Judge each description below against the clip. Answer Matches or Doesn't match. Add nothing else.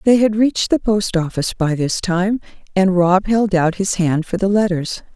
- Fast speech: Matches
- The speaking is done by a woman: Matches